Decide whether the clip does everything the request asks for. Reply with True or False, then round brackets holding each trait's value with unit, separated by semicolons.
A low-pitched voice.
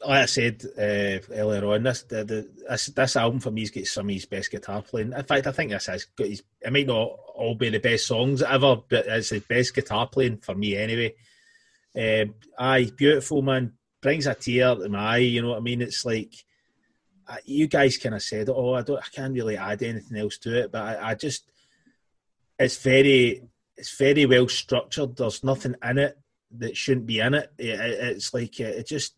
True (120 Hz)